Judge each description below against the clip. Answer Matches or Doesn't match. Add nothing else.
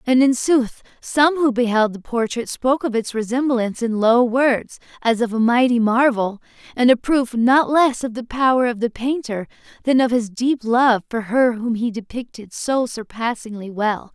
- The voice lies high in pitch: Matches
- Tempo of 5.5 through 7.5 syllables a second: Doesn't match